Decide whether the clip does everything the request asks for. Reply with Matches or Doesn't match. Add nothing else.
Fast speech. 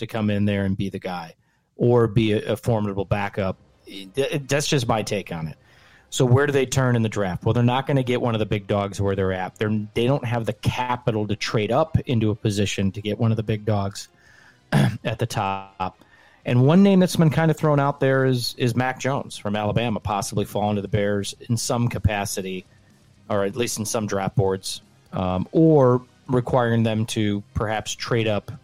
Matches